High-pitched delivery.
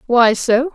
Yes: very high, 250 Hz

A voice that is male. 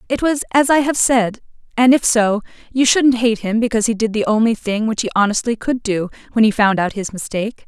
No: female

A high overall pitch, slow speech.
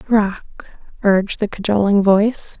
Yes: high, 205 Hz; slow, 115 wpm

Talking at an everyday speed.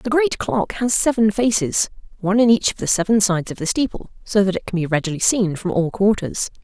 No: fast, 215 wpm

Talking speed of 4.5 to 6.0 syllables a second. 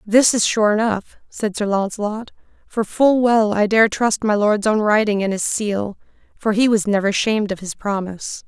Yes: 4.8 syllables/s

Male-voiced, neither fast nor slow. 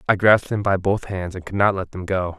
No: male; fast, 300 wpm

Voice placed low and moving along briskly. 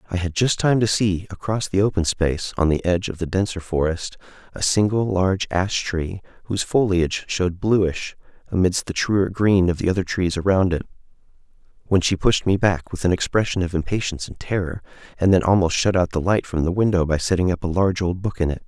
Yes: very low, 90 Hz; fast, 215 wpm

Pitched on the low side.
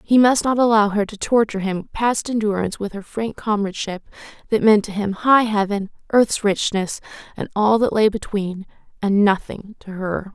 No: high, 210 Hz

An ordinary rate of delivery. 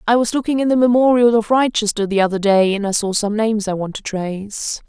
No: fast, 245 wpm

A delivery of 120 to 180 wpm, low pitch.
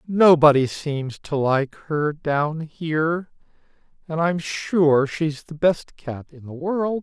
No: average, 145 wpm; medium, 155 Hz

